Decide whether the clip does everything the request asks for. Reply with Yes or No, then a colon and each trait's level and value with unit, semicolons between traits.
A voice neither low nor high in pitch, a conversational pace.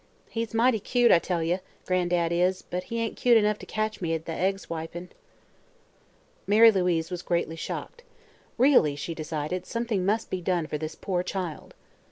Yes: medium, 180 Hz; average, 180 wpm